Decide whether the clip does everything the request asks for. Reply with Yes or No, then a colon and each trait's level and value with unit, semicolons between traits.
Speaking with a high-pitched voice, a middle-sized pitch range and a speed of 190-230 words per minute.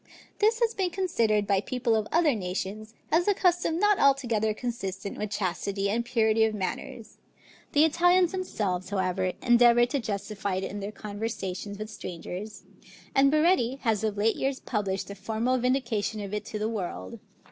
No: high, 220 Hz; average, 5.0 semitones; average, 170 wpm